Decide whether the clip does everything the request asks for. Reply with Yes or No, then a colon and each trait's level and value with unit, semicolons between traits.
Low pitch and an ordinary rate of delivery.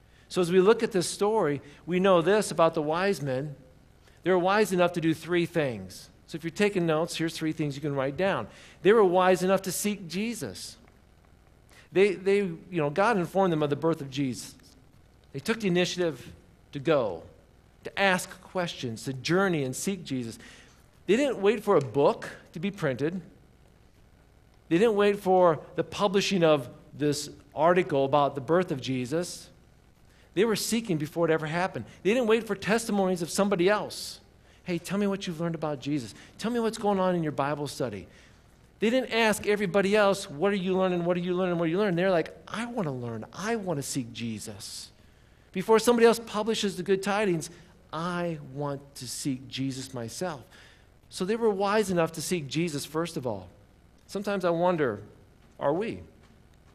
No: medium, 170 Hz; average, 190 wpm